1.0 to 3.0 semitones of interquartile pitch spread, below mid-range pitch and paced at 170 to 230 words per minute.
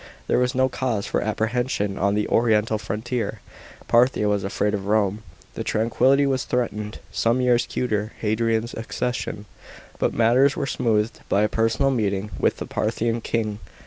No: average, 2.7 semitones; low, 115 Hz; average, 155 wpm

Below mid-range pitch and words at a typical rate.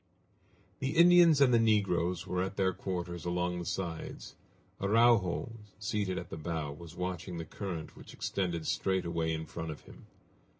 Yes: very low, 90 Hz; average, 165 wpm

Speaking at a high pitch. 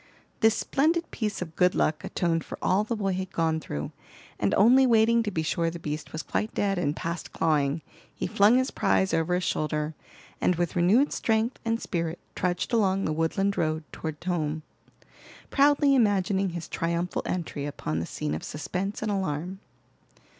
No: medium, 180 Hz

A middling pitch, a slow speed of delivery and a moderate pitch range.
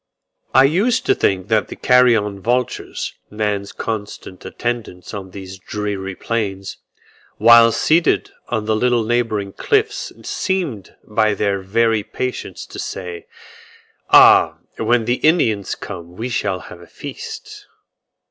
No: low, 110 Hz; slow, 130 wpm; average, 3.6 semitones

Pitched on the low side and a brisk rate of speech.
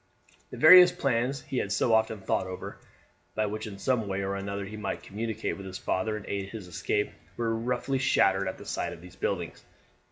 Yes: low, 105 Hz; fast, 210 wpm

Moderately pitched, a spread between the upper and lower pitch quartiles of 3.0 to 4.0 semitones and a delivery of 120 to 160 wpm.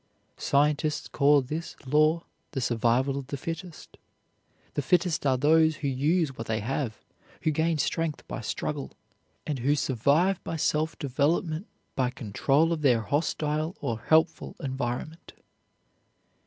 Yes: medium, 145 Hz; average, 3.3 semitones; slow, 135 wpm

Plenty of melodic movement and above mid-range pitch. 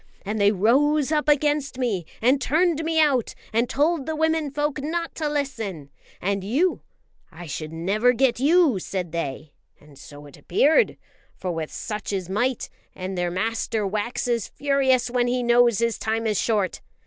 Yes: wide, 7.0 semitones; high, 240 Hz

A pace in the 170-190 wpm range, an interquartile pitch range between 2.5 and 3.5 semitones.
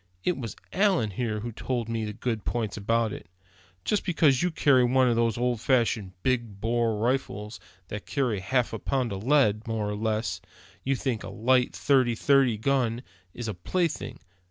Yes: average, 180 wpm; average, 3.2 semitones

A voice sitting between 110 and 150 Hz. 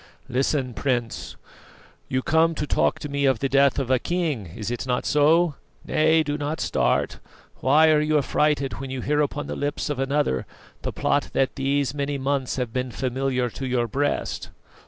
Yes: medium, 140 Hz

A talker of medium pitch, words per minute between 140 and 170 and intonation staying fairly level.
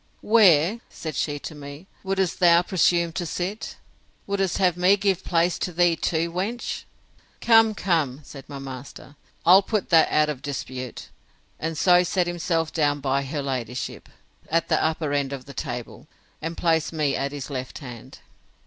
No: medium, 160 Hz; average, 165 wpm; average, 4.2 semitones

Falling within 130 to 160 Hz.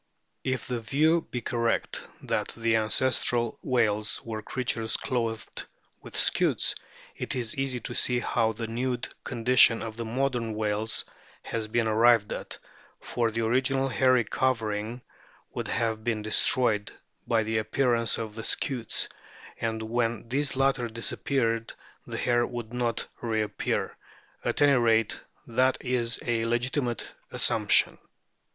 No: low, 115 Hz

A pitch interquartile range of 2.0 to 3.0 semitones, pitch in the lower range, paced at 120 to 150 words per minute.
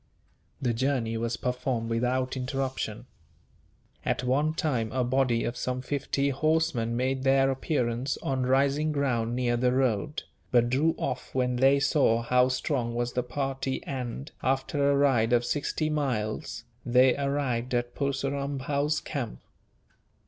Yes: narrow, 2.4 semitones; low, 130 Hz; average, 140 wpm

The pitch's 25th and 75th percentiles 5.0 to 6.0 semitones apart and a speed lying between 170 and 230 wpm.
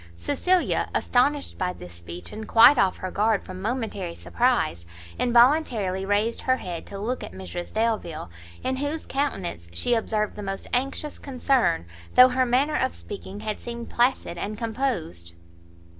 No: wide, 5.6 semitones; average, 155 wpm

